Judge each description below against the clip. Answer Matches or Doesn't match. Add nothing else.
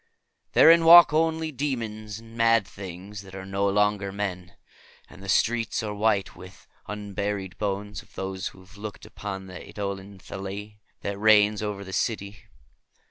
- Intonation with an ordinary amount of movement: Doesn't match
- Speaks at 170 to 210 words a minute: Doesn't match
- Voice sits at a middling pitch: Doesn't match